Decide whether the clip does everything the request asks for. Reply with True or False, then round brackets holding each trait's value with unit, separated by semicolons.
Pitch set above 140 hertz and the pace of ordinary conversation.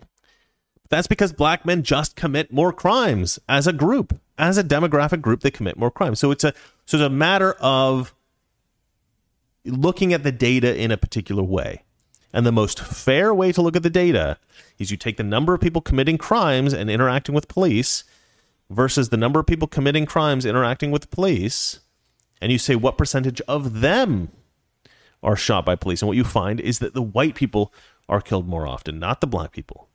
False (135 Hz; 190 wpm)